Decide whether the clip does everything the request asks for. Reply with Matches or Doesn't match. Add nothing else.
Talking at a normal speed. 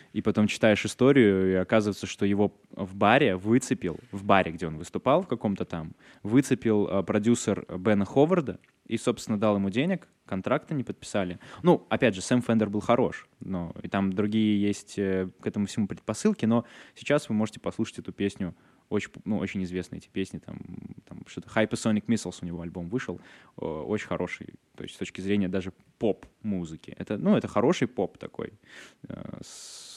Doesn't match